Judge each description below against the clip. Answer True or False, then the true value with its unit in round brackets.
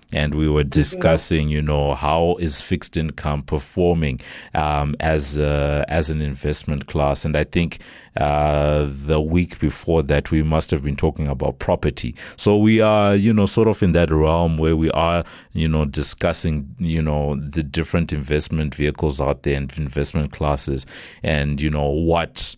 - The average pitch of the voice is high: False (75 Hz)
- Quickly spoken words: False (170 wpm)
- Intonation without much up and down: True (2.2 semitones)